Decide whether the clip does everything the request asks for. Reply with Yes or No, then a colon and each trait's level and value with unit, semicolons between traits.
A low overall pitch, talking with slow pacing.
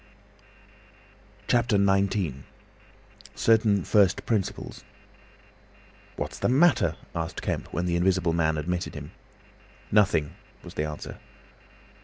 Yes: very low, 95 Hz; slow, 100 wpm